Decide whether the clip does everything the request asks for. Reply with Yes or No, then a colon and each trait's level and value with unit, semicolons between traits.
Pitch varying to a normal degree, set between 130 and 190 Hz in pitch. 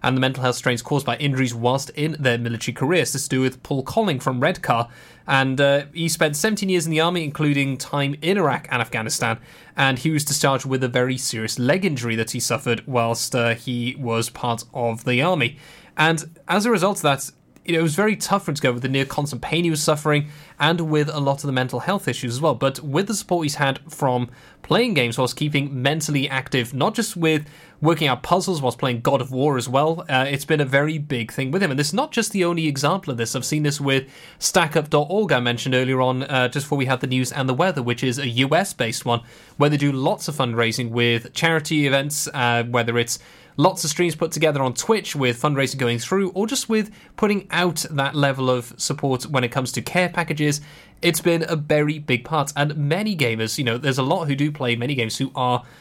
Yes: average, 4.1 semitones; medium, 140 Hz